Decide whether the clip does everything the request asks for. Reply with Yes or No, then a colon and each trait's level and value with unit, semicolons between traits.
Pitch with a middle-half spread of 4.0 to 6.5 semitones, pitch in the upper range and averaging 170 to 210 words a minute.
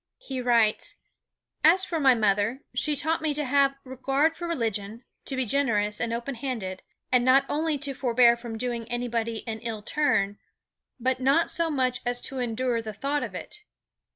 No: average, 3.6 semitones; very high, 250 Hz; average, 180 wpm